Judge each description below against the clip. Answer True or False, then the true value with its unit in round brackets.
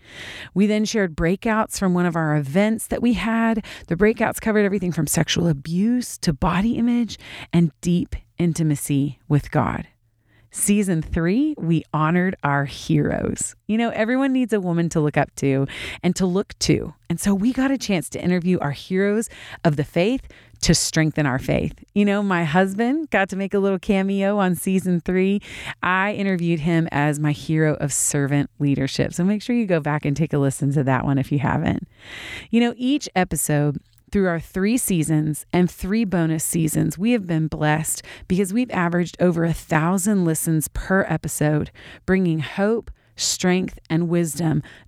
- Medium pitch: True (175 Hz)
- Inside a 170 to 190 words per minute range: True (175 wpm)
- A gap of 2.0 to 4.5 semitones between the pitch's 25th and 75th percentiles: False (4.9 semitones)